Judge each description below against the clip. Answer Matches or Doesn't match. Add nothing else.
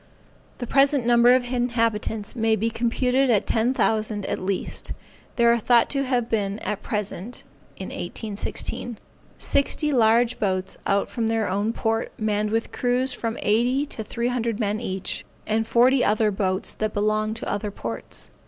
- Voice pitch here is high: Matches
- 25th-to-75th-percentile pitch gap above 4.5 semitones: Doesn't match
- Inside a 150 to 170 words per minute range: Matches